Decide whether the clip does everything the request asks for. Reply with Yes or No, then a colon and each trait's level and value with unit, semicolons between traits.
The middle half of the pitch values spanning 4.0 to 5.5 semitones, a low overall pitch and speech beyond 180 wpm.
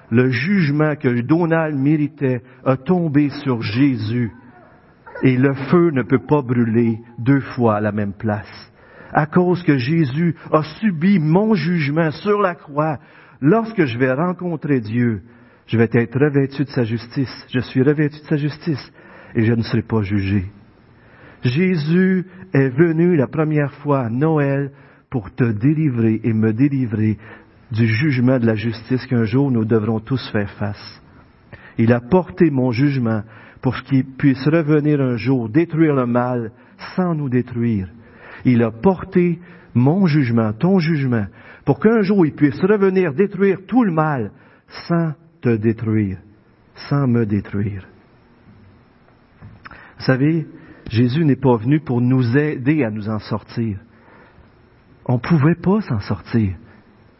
No: average, 5.1 semitones; low, 130 Hz; average, 150 wpm